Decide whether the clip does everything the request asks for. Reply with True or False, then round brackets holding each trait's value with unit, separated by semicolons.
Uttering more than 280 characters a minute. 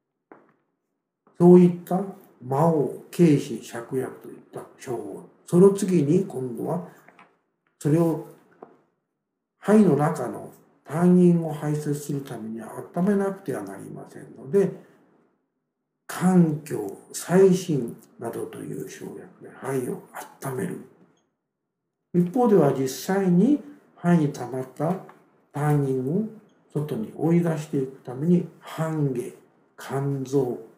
False (170 characters per minute)